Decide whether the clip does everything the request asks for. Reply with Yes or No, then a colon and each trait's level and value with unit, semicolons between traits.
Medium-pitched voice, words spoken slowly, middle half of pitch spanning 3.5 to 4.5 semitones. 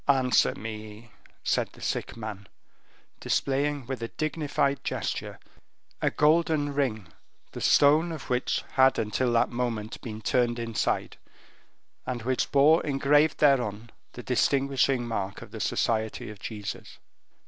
No: low, 125 Hz; slow, 130 wpm; average, 4.1 semitones